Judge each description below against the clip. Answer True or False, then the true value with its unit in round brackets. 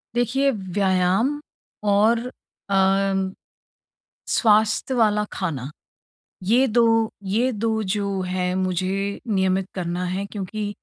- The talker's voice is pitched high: True (200 Hz)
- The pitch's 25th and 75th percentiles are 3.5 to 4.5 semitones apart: False (2.9 semitones)